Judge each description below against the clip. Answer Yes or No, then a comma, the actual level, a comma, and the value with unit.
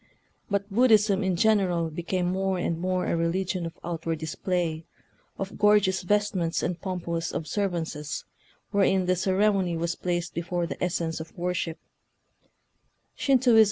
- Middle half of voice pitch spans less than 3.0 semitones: Yes, narrow, 2.4 semitones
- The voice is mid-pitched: Yes, medium, 180 Hz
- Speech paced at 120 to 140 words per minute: Yes, slow, 135 wpm